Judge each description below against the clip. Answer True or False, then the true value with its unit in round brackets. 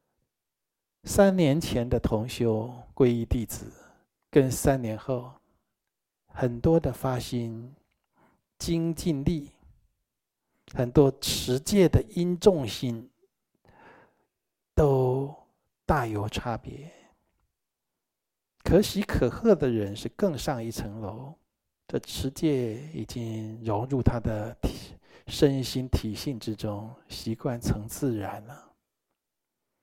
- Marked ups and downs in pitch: False (4.5 semitones)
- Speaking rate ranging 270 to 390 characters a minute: False (135 characters per minute)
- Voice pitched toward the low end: True (125 Hz)